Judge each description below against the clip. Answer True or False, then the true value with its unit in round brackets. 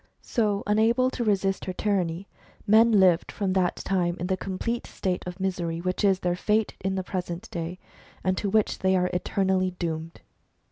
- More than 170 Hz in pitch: True (190 Hz)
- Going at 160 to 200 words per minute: True (180 wpm)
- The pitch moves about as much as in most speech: False (2.3 semitones)